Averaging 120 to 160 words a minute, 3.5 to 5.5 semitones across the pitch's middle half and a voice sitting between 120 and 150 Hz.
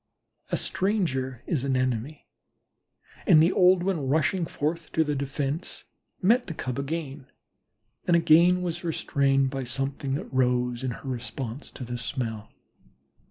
Yes: average, 145 wpm; average, 4.3 semitones; medium, 140 Hz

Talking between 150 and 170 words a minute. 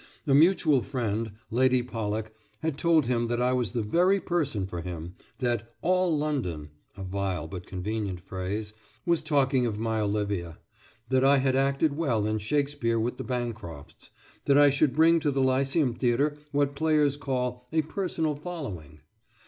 Yes: average, 165 wpm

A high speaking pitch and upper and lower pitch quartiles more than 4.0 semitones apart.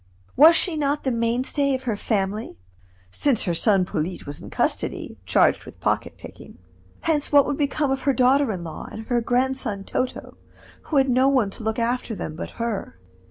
Yes: very high, 250 Hz; average, 4.4 semitones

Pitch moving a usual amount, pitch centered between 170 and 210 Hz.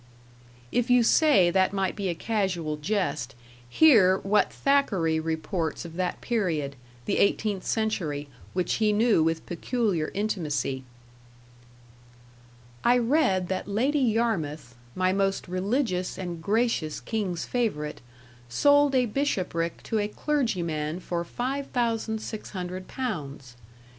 No: wide, 5.7 semitones; high, 190 Hz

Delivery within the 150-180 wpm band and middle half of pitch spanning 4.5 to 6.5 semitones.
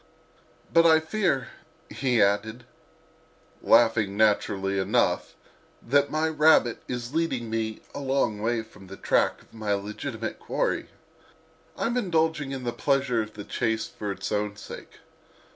No: average, 140 wpm; average, 5.0 semitones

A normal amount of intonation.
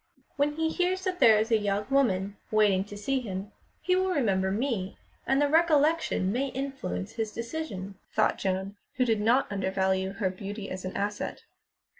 No: wide, 6.2 semitones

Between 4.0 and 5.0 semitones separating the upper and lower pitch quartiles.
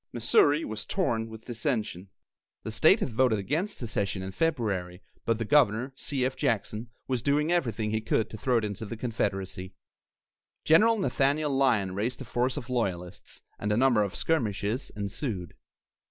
Yes: average, 4.5 semitones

